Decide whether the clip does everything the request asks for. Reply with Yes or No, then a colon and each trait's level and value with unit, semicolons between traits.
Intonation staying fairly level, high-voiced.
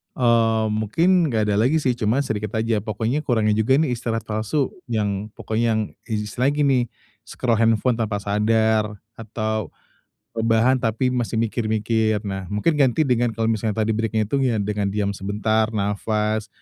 No: narrow, 2.1 semitones; low, 110 Hz